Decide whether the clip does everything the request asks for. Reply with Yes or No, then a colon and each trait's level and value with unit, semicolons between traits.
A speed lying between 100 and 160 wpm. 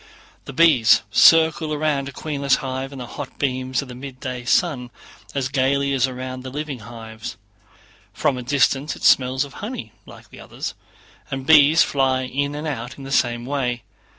No: average, 180 wpm